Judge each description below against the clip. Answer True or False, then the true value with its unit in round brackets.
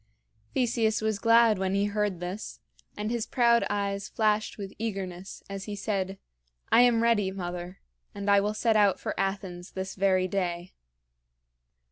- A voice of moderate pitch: False (200 Hz)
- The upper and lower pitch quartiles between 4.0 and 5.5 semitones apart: False (2.4 semitones)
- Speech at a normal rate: True (155 wpm)